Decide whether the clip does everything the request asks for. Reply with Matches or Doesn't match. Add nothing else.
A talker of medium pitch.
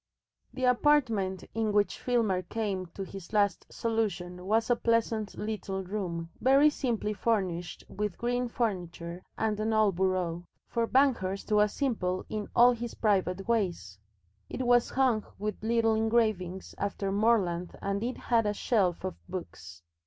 Doesn't match